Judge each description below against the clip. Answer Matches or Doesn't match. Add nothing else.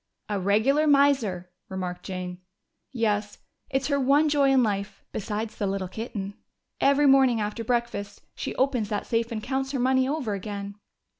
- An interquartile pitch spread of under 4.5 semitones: Doesn't match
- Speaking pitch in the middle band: Doesn't match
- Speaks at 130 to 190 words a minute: Matches